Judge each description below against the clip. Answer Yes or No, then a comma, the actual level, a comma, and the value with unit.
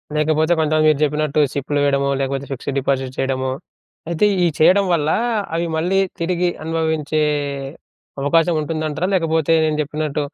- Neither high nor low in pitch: Yes, medium, 155 Hz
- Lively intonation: No, narrow, 2.5 semitones